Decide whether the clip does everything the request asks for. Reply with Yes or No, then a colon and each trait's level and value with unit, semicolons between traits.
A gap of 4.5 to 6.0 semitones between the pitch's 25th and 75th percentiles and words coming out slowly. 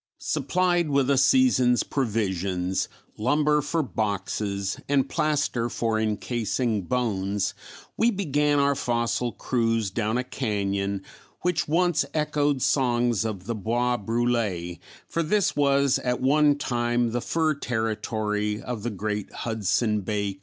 Yes: average, 5.1 semitones; slow, 130 wpm